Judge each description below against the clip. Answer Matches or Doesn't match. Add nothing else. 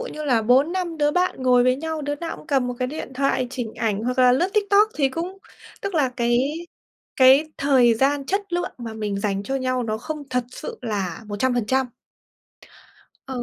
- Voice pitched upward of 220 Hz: Matches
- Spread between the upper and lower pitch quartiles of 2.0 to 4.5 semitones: Matches